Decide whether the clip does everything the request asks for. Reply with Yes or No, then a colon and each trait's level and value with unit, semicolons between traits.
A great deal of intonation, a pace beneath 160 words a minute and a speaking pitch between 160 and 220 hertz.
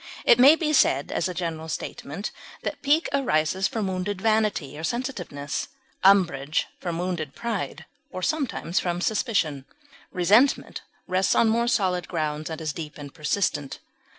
Yes: wide, 6.0 semitones; average, 150 wpm; medium, 185 Hz